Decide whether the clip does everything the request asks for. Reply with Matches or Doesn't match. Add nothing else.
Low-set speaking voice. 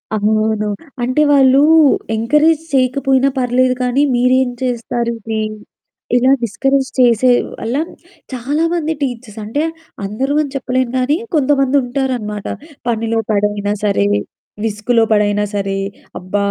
Doesn't match